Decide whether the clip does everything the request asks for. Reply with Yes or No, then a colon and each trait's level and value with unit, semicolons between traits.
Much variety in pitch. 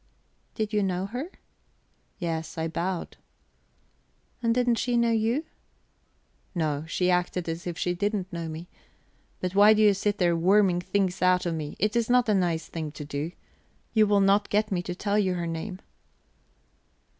No: average, 3.7 semitones